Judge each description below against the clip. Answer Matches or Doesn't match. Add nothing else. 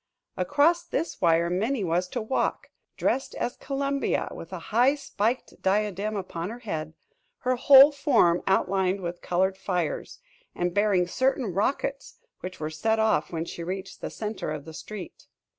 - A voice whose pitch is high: Matches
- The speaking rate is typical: Matches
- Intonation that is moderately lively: Doesn't match